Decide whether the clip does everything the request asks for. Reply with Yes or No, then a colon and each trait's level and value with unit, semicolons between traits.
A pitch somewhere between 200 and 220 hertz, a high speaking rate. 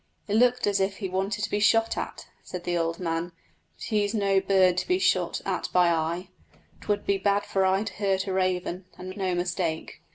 No: high, 190 Hz; fast, 215 wpm